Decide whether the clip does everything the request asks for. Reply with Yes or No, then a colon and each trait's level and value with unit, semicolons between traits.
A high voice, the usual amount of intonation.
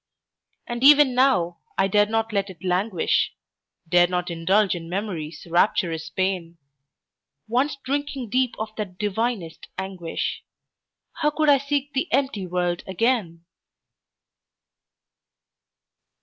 No: high, 200 Hz; wide, 6.2 semitones